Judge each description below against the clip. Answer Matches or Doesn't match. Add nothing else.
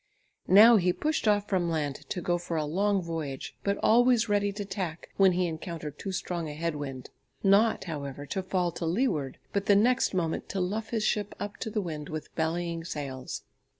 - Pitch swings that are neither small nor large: Matches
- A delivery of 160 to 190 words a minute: Doesn't match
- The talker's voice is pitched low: Doesn't match